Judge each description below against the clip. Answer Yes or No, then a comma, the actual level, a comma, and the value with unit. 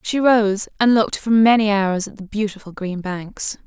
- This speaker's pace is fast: No, average, 195 wpm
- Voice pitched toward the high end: Yes, high, 210 Hz